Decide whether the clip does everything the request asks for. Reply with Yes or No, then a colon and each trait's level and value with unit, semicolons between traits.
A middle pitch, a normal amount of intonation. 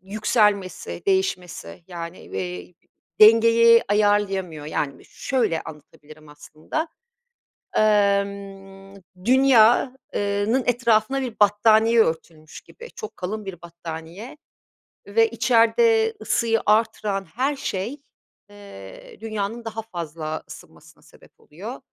No: high, 205 Hz; average, 5.0 semitones